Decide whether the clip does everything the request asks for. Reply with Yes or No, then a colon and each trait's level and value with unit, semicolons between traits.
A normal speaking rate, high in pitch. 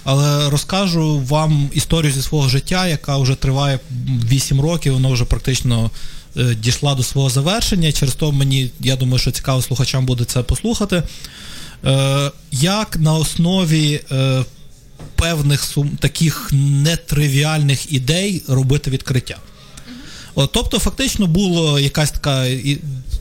No: average, 130 wpm; medium, 140 Hz